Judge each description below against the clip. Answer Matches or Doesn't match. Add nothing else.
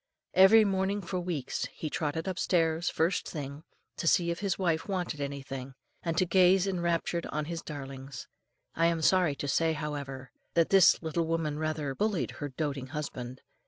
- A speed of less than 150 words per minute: Doesn't match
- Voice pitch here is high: Doesn't match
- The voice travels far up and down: Doesn't match